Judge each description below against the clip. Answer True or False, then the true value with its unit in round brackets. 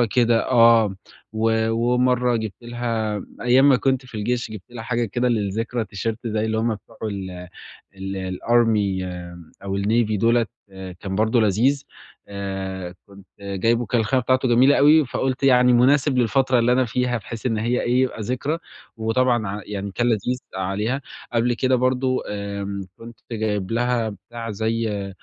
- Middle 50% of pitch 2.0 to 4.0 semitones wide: True (3.2 semitones)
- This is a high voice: False (115 Hz)